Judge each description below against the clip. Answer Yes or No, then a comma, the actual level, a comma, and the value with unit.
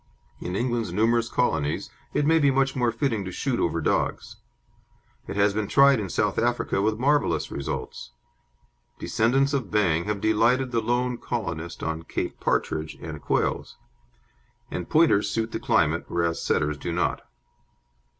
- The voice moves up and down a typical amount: No, wide, 6.1 semitones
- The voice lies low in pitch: Yes, low, 110 Hz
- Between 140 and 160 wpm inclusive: Yes, average, 150 wpm